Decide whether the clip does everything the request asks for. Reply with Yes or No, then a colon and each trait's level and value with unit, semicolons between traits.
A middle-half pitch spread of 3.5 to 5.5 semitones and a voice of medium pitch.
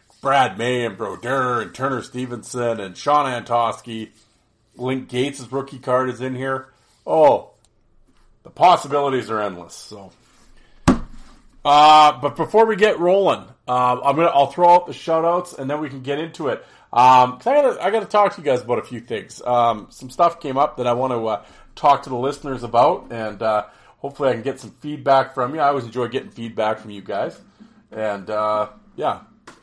No: average, 3.9 semitones; low, 130 Hz